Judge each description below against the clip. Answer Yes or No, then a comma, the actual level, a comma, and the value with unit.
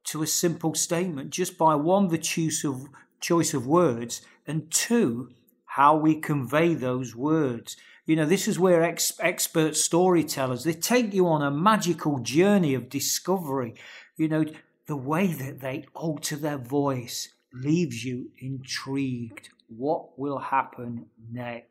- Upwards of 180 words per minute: No, average, 145 wpm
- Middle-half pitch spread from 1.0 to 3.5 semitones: No, average, 3.9 semitones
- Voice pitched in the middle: Yes, medium, 155 Hz